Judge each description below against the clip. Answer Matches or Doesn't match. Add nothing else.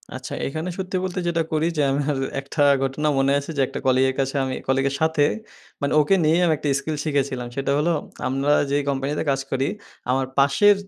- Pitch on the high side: Doesn't match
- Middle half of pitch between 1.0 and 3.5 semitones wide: Matches